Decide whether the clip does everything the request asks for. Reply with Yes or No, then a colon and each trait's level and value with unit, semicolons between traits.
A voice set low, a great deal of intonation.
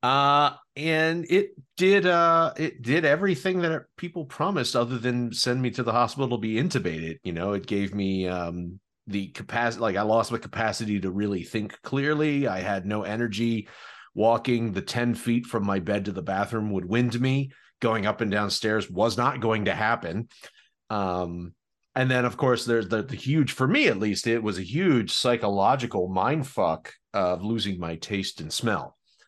No: low, 115 Hz; average, 4.6 semitones